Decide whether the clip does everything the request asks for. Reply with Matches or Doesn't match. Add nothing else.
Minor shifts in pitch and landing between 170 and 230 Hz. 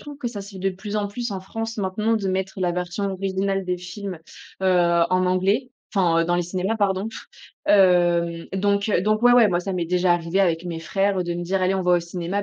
Matches